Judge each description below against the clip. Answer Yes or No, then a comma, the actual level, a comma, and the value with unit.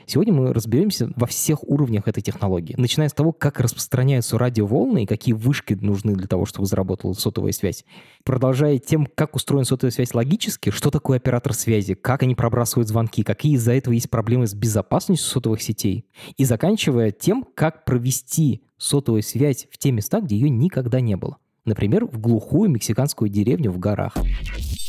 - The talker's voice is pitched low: Yes, low, 120 Hz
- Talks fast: Yes, fast, 170 wpm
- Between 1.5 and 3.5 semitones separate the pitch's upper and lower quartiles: No, average, 4.2 semitones